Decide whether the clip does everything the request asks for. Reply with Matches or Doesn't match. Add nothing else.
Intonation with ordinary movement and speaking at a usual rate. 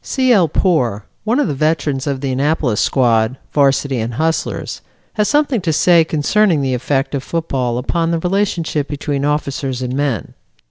Matches